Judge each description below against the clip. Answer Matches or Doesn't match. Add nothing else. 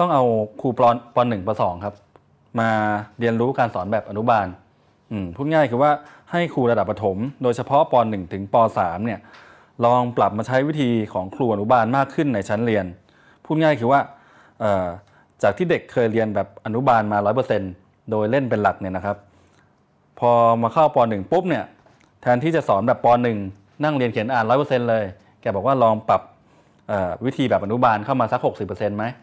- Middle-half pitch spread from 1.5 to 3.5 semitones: Doesn't match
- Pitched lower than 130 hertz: Matches